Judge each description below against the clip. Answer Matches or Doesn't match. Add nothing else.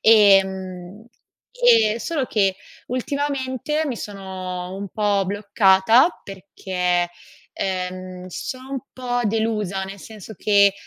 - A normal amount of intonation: Matches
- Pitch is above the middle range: Matches